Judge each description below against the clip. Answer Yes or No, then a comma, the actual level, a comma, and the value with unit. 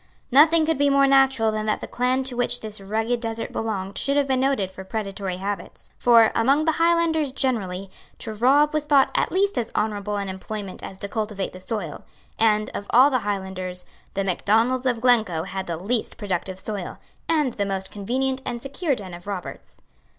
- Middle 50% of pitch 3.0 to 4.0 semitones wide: No, average, 5.3 semitones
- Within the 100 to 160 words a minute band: No, average, 195 wpm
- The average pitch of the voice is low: No, high, 225 Hz